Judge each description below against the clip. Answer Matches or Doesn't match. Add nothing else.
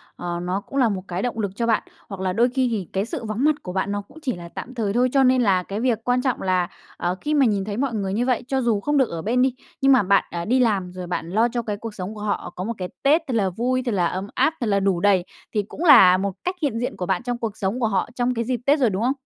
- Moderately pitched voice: Doesn't match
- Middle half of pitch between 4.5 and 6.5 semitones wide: Matches